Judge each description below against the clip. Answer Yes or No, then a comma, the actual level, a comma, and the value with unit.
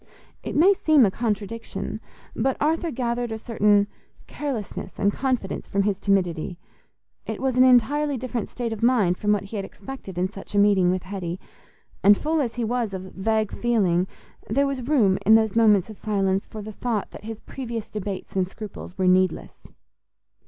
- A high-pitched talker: Yes, high, 215 Hz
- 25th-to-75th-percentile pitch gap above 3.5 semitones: Yes, average, 4.0 semitones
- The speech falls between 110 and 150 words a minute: No, average, 180 wpm